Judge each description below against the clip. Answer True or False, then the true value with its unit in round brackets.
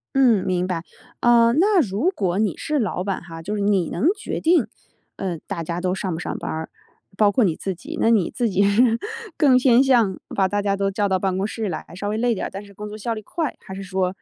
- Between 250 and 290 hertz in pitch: False (200 Hz)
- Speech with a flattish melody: False (3.7 semitones)